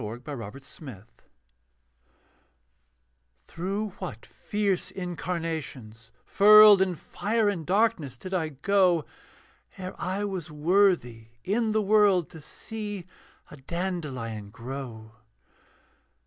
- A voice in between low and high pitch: Yes, medium, 175 Hz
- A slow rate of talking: Yes, slow, 100 wpm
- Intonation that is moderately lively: No, wide, 7.1 semitones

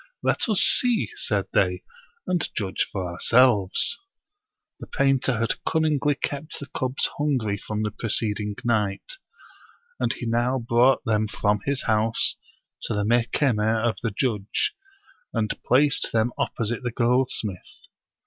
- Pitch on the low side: Yes, low, 115 Hz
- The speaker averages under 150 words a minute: Yes, average, 140 wpm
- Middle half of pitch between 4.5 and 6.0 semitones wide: No, average, 4.0 semitones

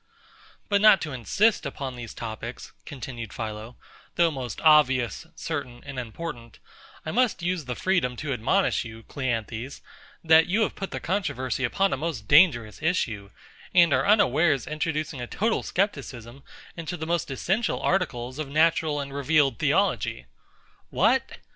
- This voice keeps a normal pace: Yes, average, 150 wpm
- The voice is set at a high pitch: No, medium, 140 Hz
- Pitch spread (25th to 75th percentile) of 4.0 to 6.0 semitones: Yes, wide, 5.6 semitones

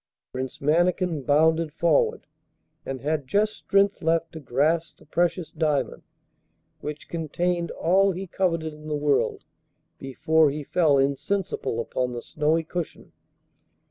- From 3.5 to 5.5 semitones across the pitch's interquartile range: No, average, 3.1 semitones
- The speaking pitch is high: No, medium, 160 Hz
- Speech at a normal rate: No, slow, 130 wpm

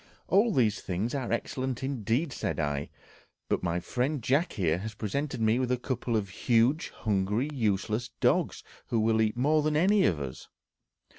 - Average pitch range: Yes, average, 4.9 semitones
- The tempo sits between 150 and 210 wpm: Yes, average, 170 wpm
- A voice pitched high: No, low, 115 Hz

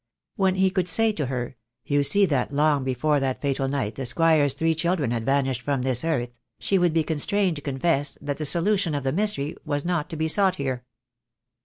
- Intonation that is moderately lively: Yes, average, 4.2 semitones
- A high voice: No, medium, 145 Hz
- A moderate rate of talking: No, fast, 210 wpm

